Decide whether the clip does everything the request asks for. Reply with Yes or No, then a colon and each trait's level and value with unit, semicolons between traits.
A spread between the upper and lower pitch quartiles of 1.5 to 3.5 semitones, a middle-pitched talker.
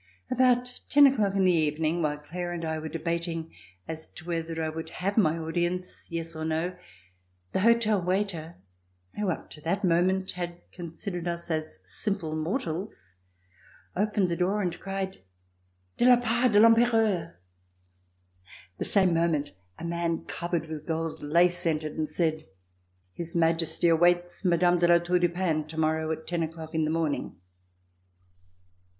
Yes: average, 2.7 semitones; medium, 170 Hz